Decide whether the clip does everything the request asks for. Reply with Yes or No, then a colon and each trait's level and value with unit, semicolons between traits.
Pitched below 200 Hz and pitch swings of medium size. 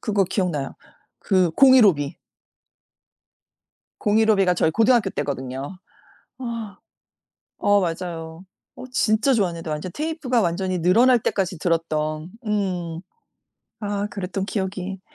Yes: high, 190 Hz; average, 4.2 semitones